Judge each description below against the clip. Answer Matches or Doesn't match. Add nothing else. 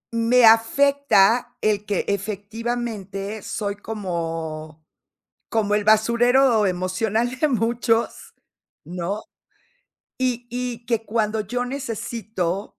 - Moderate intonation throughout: Matches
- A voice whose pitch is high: Matches